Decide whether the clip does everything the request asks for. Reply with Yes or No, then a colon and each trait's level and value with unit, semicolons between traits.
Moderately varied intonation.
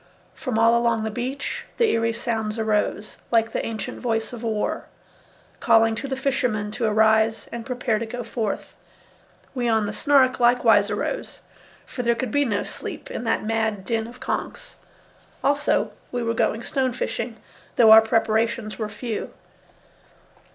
No: narrow, 2.0 semitones